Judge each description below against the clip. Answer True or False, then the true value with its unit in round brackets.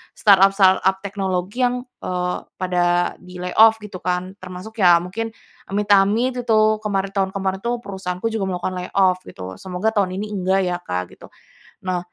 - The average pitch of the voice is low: False (190 Hz)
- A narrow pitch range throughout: True (2.3 semitones)